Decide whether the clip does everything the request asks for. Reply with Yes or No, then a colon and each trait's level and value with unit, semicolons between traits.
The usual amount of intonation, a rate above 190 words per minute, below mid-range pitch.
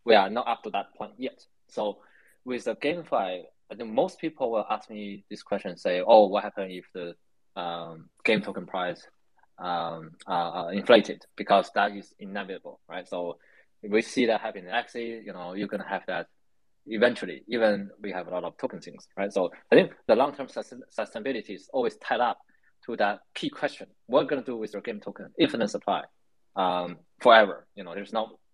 Yes: average, 3.6 semitones; average, 200 wpm; low, 100 Hz